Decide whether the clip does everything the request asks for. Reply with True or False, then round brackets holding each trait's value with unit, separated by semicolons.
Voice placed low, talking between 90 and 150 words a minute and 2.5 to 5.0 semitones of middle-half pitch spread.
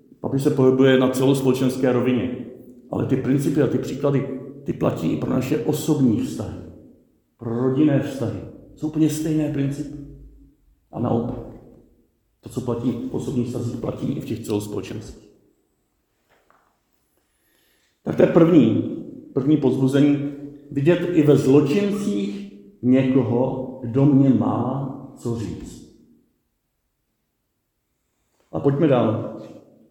True (130 Hz; 115 wpm; 2.8 semitones)